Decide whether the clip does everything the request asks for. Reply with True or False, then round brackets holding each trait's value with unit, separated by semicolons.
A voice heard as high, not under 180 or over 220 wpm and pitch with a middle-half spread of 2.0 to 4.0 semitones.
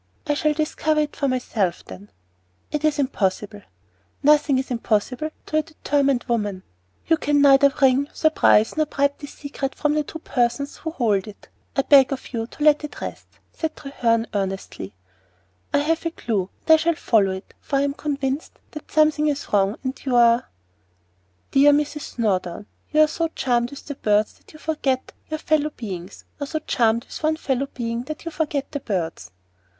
False (275 Hz; 185 wpm; 5.1 semitones)